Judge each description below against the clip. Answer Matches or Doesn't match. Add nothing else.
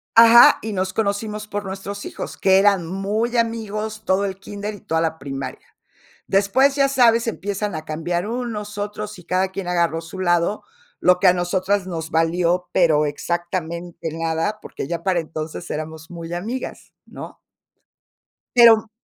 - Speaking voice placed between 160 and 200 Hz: Matches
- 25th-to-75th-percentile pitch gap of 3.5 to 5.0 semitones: Matches